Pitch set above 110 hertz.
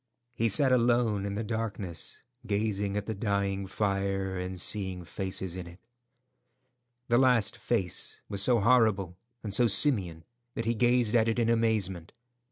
No: low, 100 Hz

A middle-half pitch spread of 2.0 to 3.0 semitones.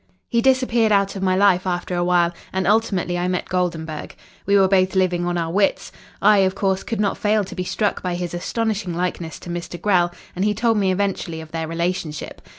Yes: narrow, 2.5 semitones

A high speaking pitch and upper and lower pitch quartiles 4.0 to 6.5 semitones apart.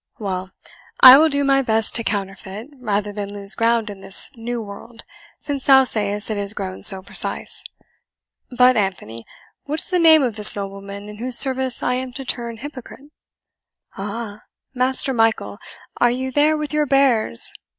Yes: high, 230 Hz; average, 4.4 semitones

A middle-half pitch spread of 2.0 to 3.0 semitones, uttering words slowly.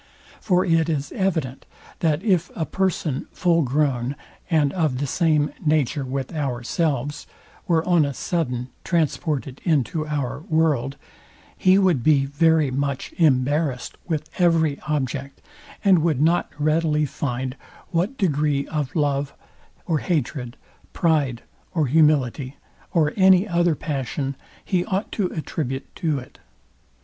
No: average, 3.4 semitones; slow, 130 wpm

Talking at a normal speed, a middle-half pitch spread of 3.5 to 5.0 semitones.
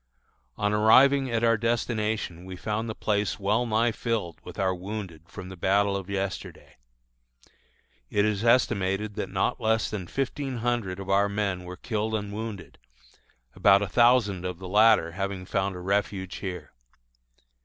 No: average, 160 wpm; average, 2.9 semitones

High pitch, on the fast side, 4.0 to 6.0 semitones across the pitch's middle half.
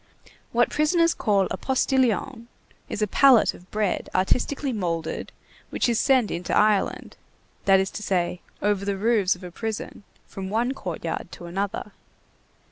No: high, 210 Hz; average, 150 wpm; average, 4.3 semitones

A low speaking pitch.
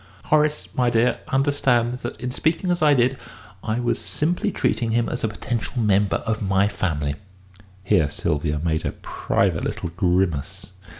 Yes: low, 115 Hz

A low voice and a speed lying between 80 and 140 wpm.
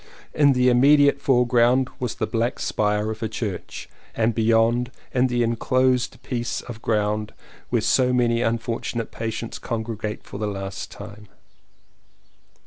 Yes: low, 115 Hz; slow, 135 wpm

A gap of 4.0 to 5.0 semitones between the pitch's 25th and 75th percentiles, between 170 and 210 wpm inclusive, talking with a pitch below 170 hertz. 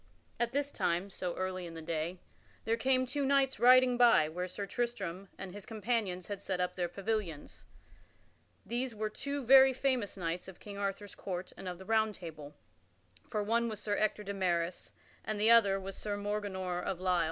No: average, 4.4 semitones; average, 190 wpm; high, 200 Hz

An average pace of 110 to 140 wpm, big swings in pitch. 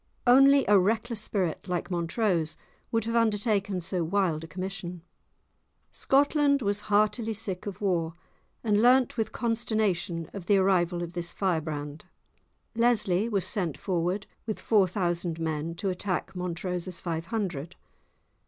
No: slow, 135 wpm; average, 3.9 semitones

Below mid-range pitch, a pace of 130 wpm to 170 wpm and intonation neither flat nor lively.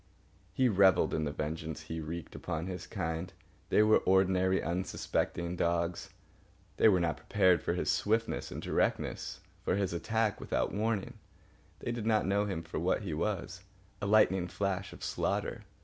Yes: very low, 95 Hz; average, 165 wpm; average, 3.2 semitones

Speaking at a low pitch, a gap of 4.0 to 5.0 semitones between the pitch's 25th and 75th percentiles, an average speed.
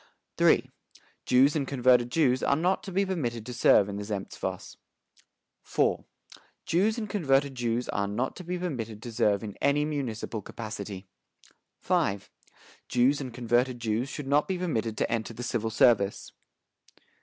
Yes: low, 125 Hz; average, 4.7 semitones; average, 155 wpm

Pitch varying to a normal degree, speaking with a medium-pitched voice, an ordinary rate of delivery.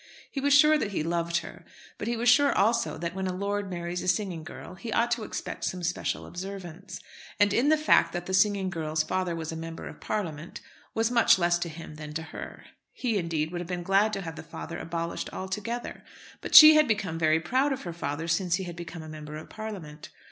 No: average, 4.4 semitones; medium, 180 Hz; fast, 225 wpm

